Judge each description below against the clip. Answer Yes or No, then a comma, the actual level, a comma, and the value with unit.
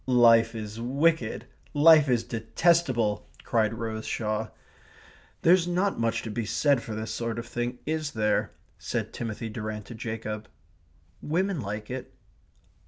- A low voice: Yes, low, 115 Hz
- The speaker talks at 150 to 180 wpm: No, average, 140 wpm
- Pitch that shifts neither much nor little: Yes, average, 4.6 semitones